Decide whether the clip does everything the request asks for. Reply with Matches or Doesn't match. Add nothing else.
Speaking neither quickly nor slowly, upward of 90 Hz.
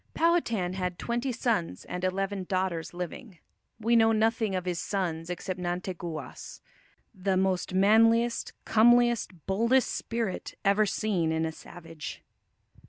Doesn't match